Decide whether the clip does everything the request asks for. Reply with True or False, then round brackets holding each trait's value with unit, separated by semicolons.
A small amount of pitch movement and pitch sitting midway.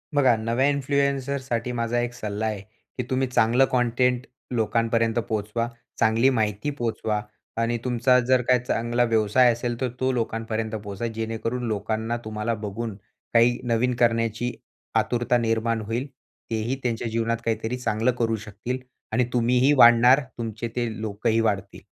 False (1.9 semitones; 115 Hz)